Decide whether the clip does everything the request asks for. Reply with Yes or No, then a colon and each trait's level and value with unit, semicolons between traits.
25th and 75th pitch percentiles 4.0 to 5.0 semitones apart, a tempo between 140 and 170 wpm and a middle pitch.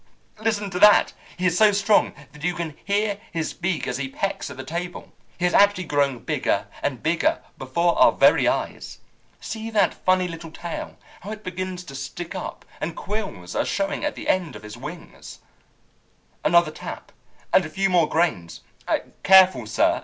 No: average, 4.3 semitones; average, 180 wpm; medium, 175 Hz